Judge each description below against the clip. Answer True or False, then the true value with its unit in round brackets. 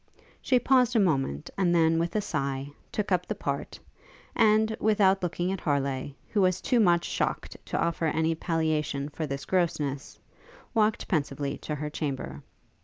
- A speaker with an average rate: True (165 wpm)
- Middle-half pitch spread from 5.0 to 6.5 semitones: True (5.3 semitones)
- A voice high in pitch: False (165 Hz)